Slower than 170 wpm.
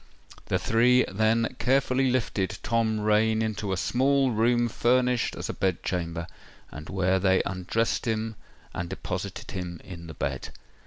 Yes: average, 150 wpm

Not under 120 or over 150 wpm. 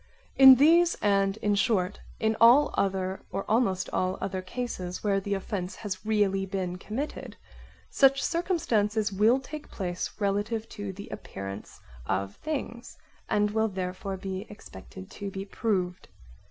Yes: average, 140 wpm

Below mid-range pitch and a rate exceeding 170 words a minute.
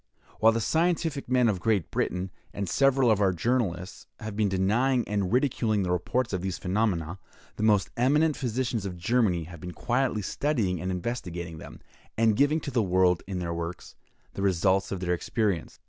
Yes: low, 100 Hz; average, 180 wpm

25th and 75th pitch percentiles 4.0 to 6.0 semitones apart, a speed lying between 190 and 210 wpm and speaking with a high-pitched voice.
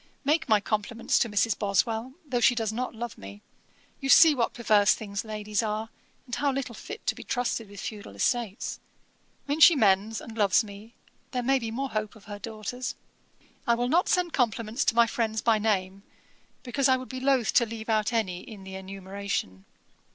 No: average, 3.2 semitones; average, 195 wpm; high, 225 Hz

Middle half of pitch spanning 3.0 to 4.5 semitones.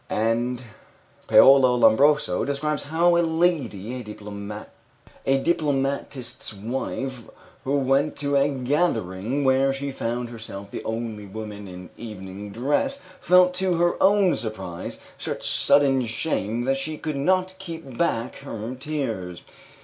No: average, 5.1 semitones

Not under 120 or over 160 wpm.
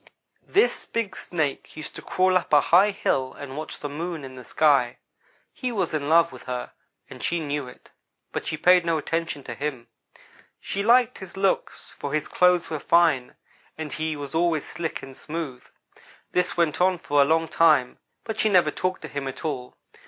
No: average, 195 wpm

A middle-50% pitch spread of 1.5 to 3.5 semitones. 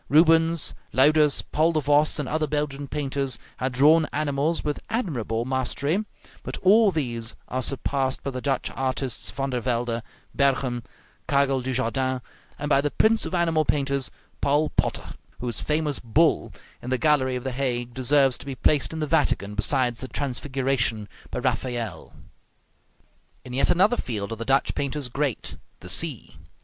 Yes: average, 3.1 semitones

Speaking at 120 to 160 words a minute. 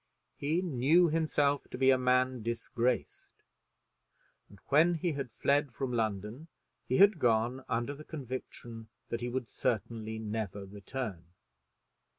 Yes: slow, 135 wpm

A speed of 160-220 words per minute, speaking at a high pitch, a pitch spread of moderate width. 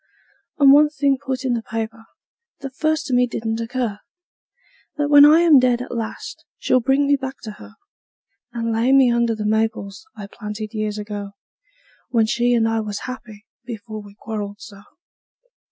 Yes: average, 175 wpm; high, 230 Hz; average, 3.5 semitones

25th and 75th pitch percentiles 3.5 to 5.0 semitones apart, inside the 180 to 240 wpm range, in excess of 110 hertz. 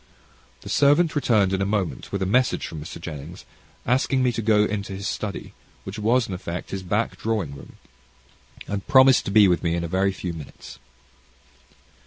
No: average, 4.3 semitones; average, 185 wpm; low, 100 Hz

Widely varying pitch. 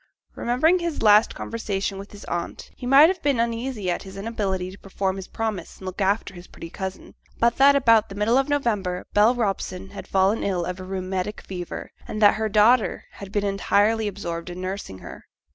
No: average, 3.3 semitones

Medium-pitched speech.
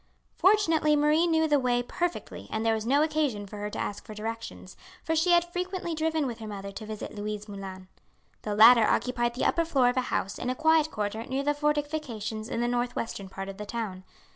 No: high, 245 Hz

